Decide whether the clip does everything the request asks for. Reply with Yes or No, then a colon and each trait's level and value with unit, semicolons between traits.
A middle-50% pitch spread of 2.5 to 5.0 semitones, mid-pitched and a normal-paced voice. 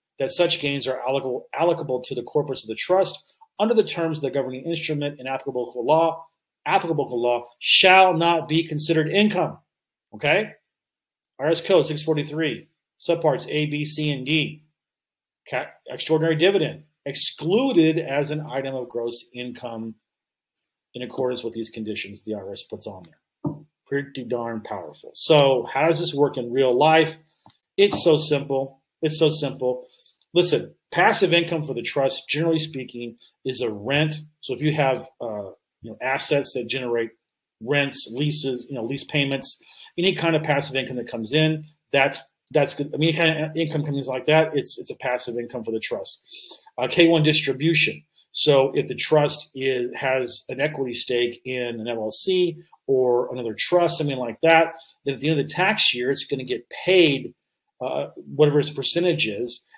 Yes: average, 4.0 semitones; medium, 145 Hz; average, 175 wpm